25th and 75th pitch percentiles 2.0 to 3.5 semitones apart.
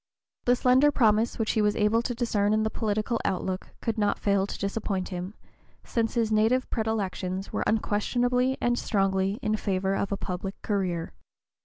Yes: average, 2.8 semitones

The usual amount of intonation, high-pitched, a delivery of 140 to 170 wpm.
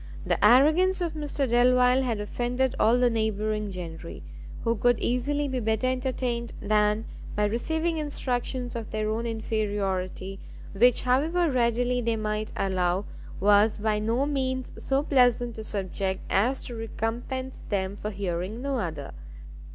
Yes: average, 3.5 semitones; high, 230 Hz; average, 145 wpm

